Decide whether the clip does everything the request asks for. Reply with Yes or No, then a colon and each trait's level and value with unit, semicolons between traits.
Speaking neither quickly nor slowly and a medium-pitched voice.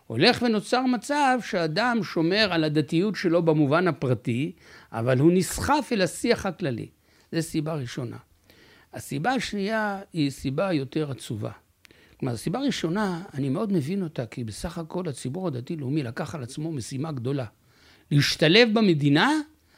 Yes: average, 135 wpm; medium, 165 Hz